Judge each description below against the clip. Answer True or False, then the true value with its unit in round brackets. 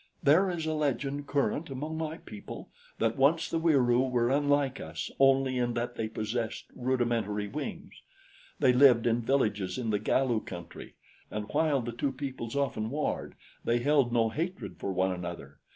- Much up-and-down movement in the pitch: False (4.1 semitones)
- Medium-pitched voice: False (125 Hz)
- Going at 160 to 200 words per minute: True (170 wpm)